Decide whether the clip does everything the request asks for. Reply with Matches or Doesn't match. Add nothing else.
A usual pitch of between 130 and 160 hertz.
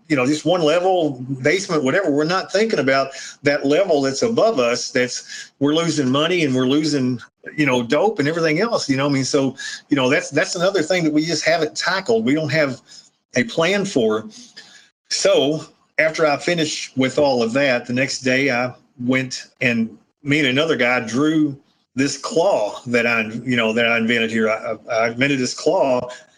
Matches